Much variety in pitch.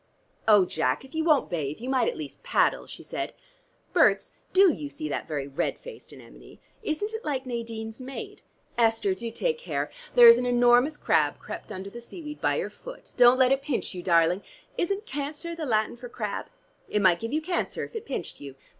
Yes: wide, 6.7 semitones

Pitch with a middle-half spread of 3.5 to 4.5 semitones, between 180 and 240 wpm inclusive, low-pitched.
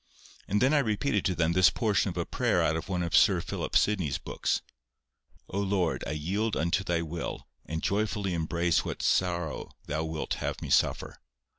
Yes: average, 3.8 semitones; average, 185 wpm; very low, 90 Hz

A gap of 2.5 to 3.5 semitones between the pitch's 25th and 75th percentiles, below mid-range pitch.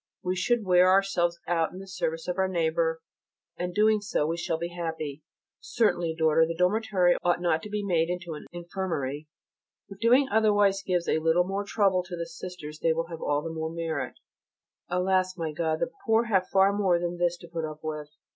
No: average, 2.8 semitones; medium, 175 Hz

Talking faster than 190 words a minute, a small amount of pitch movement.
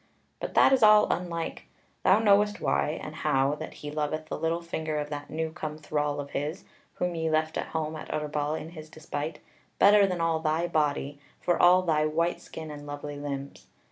Yes: average, 200 wpm; narrow, 2.3 semitones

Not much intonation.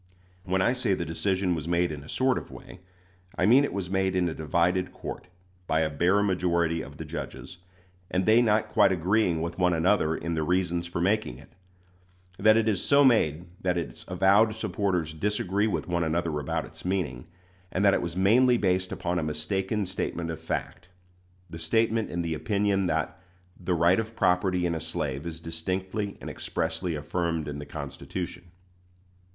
No: average, 3.1 semitones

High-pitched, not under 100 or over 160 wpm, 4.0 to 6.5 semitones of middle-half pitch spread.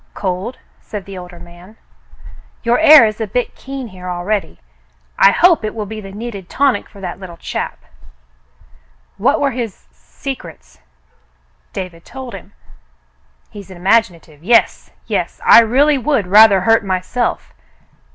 Yes: high, 210 Hz; average, 155 wpm; average, 4.5 semitones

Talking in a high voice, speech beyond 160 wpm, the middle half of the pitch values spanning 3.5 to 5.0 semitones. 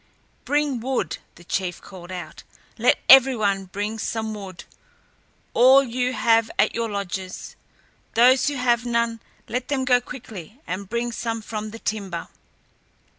No: high, 225 Hz; average, 145 wpm; average, 3.8 semitones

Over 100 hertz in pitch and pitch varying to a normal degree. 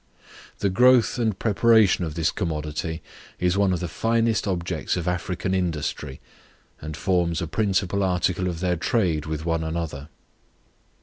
No: very low, 90 Hz; average, 3.4 semitones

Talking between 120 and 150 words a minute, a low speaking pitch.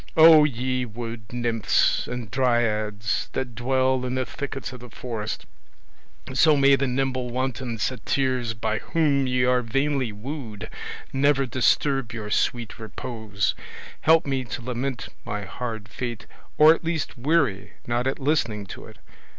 Yes: average, 145 wpm; low, 125 Hz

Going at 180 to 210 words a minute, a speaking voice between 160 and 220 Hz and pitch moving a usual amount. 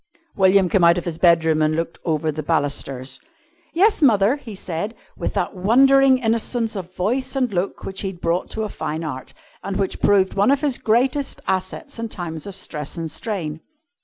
No: average, 190 wpm; high, 190 Hz; wide, 5.7 semitones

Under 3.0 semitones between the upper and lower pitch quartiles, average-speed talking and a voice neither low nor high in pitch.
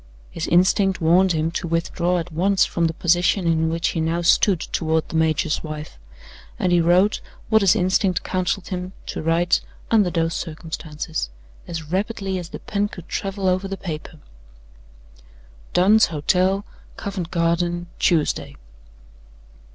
Yes: narrow, 2.5 semitones; average, 145 wpm; medium, 175 Hz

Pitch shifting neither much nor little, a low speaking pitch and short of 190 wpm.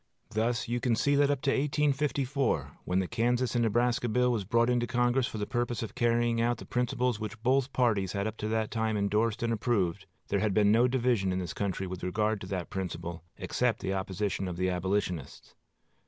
No: average, 3.6 semitones; low, 115 Hz; fast, 205 wpm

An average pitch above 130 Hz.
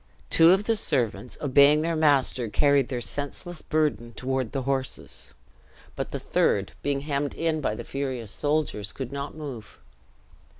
Yes: medium, 140 Hz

